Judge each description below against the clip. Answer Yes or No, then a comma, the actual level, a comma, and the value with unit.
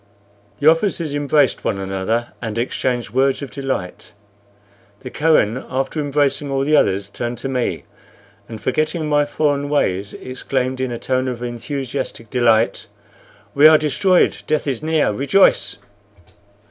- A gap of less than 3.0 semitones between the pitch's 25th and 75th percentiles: No, average, 3.6 semitones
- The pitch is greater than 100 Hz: Yes, low, 135 Hz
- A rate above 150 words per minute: No, average, 140 wpm